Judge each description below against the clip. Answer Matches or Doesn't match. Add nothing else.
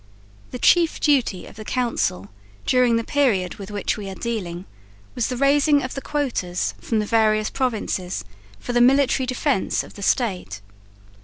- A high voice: Matches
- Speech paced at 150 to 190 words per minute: Matches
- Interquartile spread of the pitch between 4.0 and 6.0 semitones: Matches